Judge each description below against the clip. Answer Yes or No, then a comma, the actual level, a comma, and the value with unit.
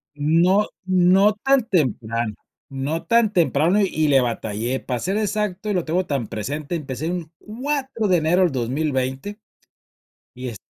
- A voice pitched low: No, medium, 165 Hz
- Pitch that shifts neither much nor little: No, wide, 6.9 semitones